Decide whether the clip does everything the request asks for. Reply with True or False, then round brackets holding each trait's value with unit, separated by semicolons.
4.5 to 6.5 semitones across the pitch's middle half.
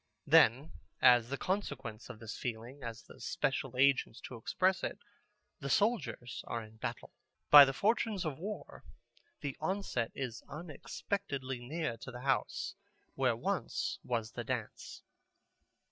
True (5.4 semitones)